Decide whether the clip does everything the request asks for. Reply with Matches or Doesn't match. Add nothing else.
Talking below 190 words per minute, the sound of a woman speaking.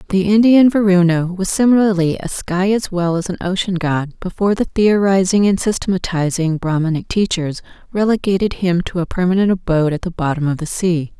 Matches